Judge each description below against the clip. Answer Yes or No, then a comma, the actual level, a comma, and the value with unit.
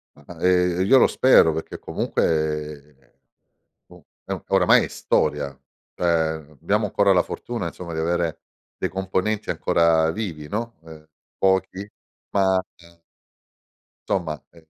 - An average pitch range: Yes, average, 3.2 semitones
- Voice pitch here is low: Yes, very low, 85 Hz